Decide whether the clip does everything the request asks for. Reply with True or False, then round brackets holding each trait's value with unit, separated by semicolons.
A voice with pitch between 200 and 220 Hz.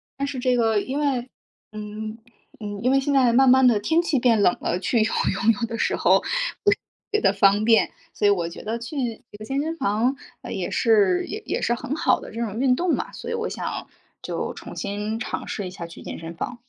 False (235 Hz)